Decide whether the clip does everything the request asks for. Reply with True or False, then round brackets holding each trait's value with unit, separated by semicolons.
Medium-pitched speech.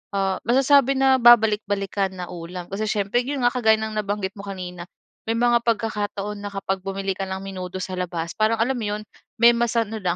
False (205 Hz)